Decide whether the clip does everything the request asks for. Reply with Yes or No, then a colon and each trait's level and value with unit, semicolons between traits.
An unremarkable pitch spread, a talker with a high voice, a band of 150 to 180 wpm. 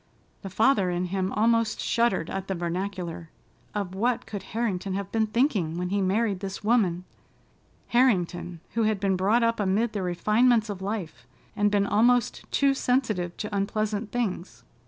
Yes: average, 3.6 semitones; high, 205 Hz; average, 155 wpm